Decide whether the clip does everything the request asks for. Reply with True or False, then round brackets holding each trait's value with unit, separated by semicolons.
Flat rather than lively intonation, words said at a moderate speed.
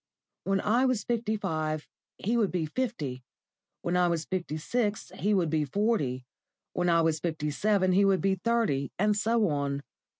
False (5.5 semitones; 175 wpm)